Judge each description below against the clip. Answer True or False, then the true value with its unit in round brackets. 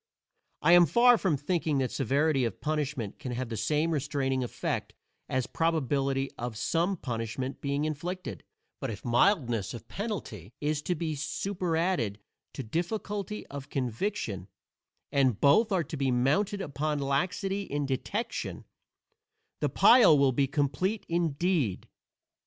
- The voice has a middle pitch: True (145 Hz)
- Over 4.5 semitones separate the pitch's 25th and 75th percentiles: True (5.1 semitones)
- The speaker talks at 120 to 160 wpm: True (135 wpm)